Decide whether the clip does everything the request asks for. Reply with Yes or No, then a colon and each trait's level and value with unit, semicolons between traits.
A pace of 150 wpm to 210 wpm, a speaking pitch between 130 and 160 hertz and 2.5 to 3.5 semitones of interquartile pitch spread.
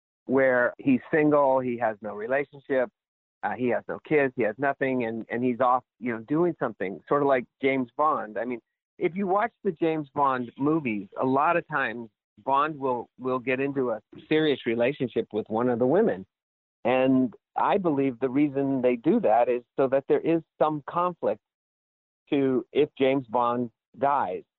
Yes: average, 180 wpm; low, 135 Hz; average, 3.2 semitones